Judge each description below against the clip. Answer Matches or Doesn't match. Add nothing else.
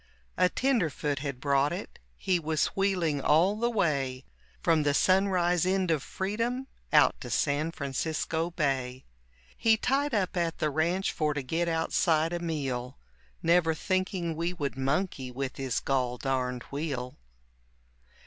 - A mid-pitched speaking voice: Matches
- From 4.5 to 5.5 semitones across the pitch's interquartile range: Matches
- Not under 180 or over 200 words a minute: Doesn't match